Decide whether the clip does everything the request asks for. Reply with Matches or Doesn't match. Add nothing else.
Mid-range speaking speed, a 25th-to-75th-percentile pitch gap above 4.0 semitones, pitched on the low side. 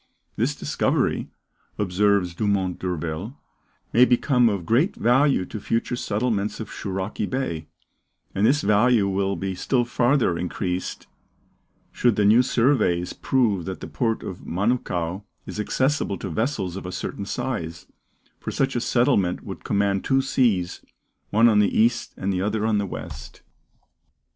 Matches